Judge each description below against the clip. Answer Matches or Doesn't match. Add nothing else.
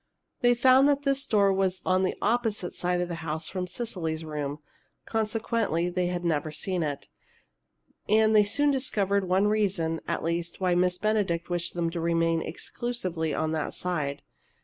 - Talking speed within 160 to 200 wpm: Matches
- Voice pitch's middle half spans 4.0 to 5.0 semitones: Matches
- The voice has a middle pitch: Matches